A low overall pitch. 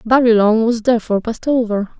No: high, 225 Hz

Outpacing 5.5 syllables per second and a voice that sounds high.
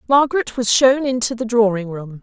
No: 5.4 syllables/s; high, 235 Hz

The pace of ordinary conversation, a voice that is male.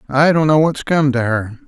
No: fast, 250 wpm; male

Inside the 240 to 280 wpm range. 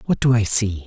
Yes: fast, 275 wpm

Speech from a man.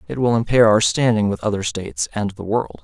Yes: male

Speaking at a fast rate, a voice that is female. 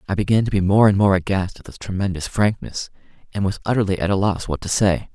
No: fast, 245 wpm; male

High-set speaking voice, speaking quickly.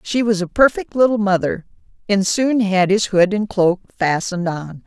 No: high, 200 Hz; average, 185 wpm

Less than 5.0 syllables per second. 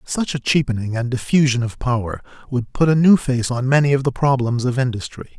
No: 5.7 syllables/s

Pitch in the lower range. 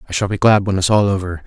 Yes: very low, 95 Hz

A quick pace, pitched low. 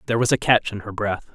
Yes: fast, 315 wpm; low, 110 Hz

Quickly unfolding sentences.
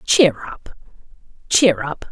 No: slow, 115 wpm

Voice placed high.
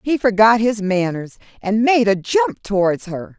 Yes: high, 210 Hz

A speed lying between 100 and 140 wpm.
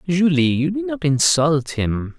Yes: slow, 135 wpm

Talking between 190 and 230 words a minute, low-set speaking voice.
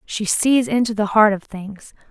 No: average, 200 wpm; high, 210 Hz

